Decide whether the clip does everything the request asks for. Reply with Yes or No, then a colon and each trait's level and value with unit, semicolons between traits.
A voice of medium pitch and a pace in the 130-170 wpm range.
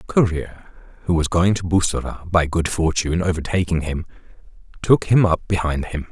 No: very low, 85 Hz; average, 165 wpm